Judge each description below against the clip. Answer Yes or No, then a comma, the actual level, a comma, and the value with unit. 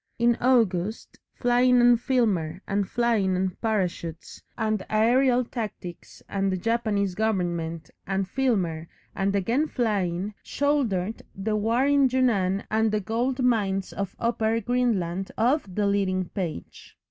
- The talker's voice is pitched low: No, high, 215 Hz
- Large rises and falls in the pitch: No, average, 4.2 semitones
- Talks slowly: Yes, slow, 130 wpm